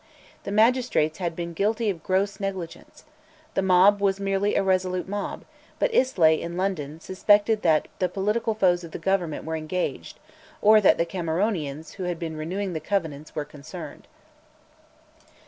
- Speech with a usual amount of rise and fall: Yes, average, 3.6 semitones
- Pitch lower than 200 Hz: Yes, medium, 185 Hz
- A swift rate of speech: No, average, 160 wpm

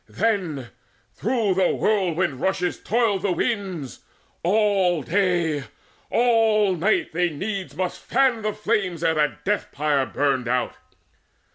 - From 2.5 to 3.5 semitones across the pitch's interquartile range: No, average, 4.7 semitones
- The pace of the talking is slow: Yes, slow, 125 wpm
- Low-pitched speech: No, medium, 185 Hz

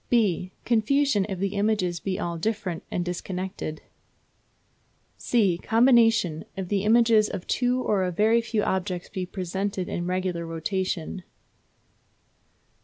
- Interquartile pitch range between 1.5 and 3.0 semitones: No, average, 3.6 semitones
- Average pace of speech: No, slow, 125 wpm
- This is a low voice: No, high, 190 Hz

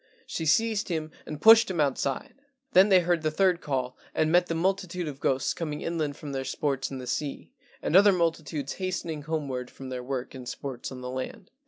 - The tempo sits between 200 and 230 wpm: Yes, fast, 205 wpm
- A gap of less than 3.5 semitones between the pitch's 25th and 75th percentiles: No, average, 4.7 semitones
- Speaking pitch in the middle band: Yes, medium, 155 Hz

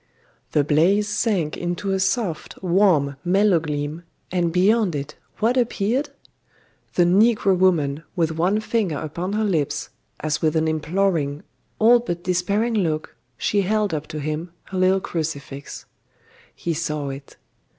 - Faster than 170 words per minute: No, average, 140 wpm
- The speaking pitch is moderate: Yes, medium, 175 Hz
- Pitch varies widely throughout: No, average, 4.6 semitones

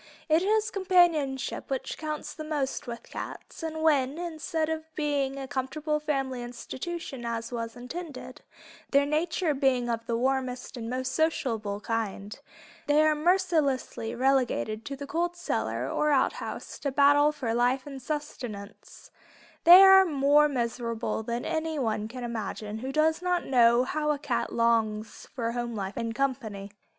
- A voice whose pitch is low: No, very high, 270 Hz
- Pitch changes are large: No, average, 4.6 semitones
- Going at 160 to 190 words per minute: No, average, 150 wpm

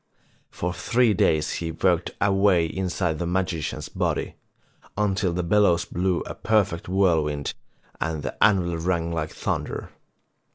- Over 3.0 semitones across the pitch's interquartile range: No, narrow, 2.6 semitones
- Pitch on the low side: Yes, very low, 90 Hz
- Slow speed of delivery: Yes, slow, 130 wpm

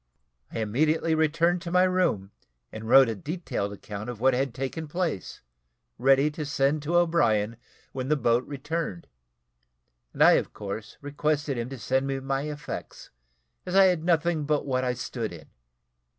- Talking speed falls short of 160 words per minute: No, average, 165 wpm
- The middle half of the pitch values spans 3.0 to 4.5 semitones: No, average, 5.0 semitones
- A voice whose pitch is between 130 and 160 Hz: Yes, medium, 140 Hz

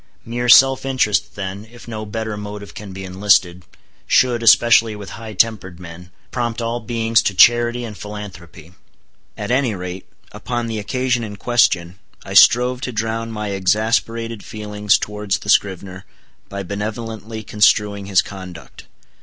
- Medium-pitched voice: No, low, 105 Hz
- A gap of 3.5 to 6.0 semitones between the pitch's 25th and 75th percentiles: No, average, 2.8 semitones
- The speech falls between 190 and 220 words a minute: No, average, 145 wpm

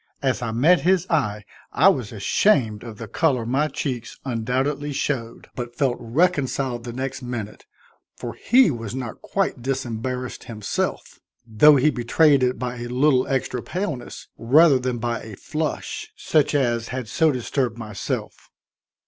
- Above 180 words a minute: No, average, 150 wpm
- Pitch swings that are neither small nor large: Yes, average, 3.6 semitones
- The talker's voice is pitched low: Yes, low, 125 Hz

